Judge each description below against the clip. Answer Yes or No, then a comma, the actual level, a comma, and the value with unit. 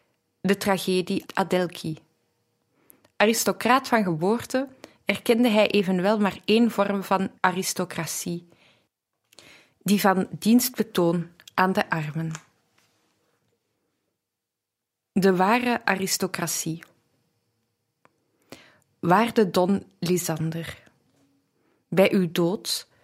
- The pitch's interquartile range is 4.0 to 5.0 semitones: No, average, 3.4 semitones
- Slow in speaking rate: Yes, slow, 75 wpm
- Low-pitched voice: No, medium, 185 Hz